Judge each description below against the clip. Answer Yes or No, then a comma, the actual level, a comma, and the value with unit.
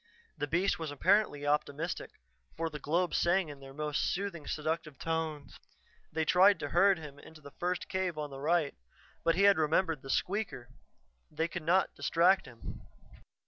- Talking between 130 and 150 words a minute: No, average, 170 wpm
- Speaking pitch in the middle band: Yes, medium, 160 Hz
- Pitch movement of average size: Yes, average, 3.4 semitones